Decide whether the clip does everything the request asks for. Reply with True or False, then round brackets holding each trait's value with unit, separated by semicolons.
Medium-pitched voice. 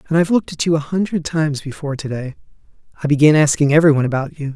True (150 Hz)